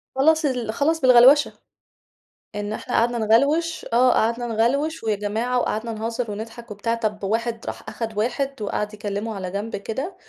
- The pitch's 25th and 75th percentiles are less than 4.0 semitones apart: Yes, average, 3.1 semitones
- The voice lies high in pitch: Yes, high, 230 Hz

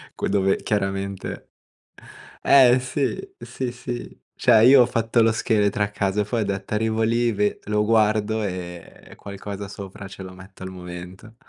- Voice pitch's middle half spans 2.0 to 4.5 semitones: Yes, narrow, 2.6 semitones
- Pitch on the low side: Yes, low, 105 Hz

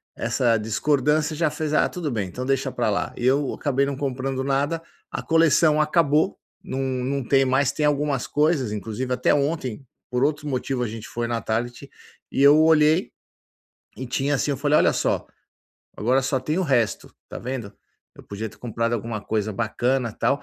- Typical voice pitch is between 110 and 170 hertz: Yes, low, 135 Hz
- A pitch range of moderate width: Yes, average, 3.7 semitones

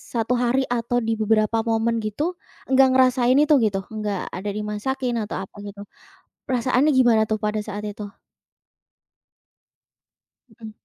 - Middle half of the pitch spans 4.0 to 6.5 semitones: No, average, 3.1 semitones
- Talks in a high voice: Yes, high, 225 Hz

